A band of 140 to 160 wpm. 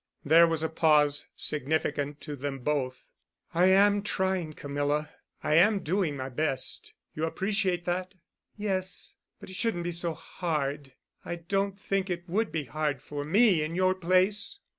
Yes: average, 155 wpm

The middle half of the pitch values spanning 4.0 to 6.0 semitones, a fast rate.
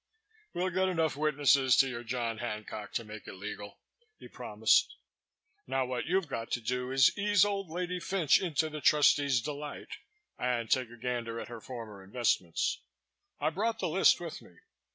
No: wide, 5.5 semitones; average, 175 wpm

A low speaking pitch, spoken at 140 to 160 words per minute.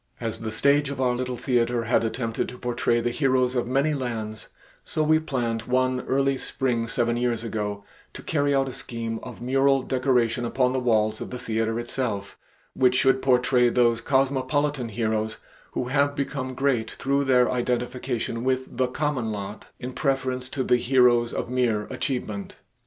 No: low, 125 Hz; average, 170 wpm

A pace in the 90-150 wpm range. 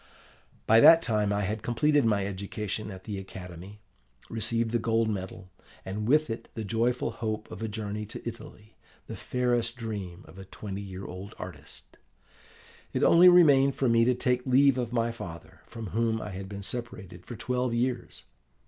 No: average, 175 wpm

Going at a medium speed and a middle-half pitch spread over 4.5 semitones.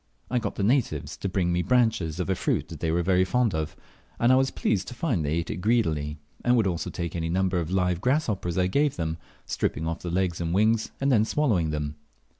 No: fast, 230 wpm; wide, 5.5 semitones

